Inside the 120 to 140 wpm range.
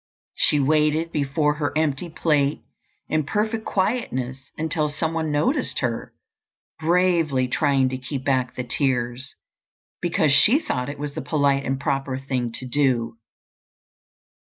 Yes: slow, 135 wpm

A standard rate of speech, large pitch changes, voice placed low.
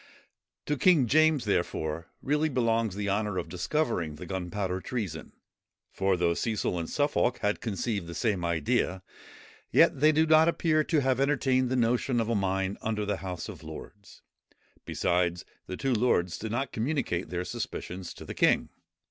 Yes: average, 165 wpm; wide, 6.4 semitones; low, 105 Hz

